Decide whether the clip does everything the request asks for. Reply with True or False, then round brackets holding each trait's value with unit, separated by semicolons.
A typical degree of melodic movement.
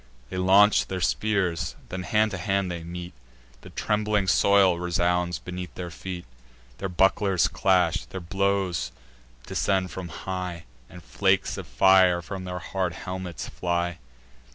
False (1.7 semitones)